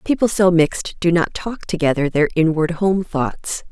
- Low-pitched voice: No, medium, 170 Hz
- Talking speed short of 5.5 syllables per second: Yes, 4.6 syllables/s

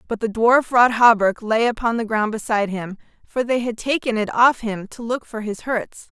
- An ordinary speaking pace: No, fast, 225 wpm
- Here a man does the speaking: No, female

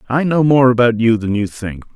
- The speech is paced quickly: Yes, fast, 245 wpm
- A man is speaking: Yes, male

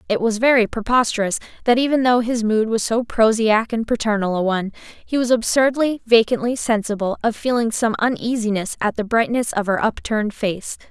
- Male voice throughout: No, female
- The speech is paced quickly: No, average, 175 wpm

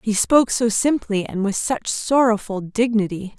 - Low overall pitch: No, high, 220 Hz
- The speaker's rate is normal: Yes, average, 160 wpm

